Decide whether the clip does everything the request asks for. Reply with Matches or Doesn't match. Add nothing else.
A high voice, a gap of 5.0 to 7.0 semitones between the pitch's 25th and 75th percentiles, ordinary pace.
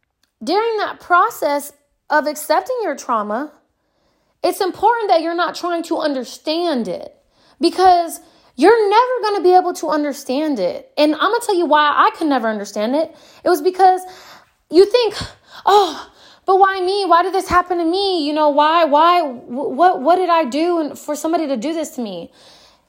Doesn't match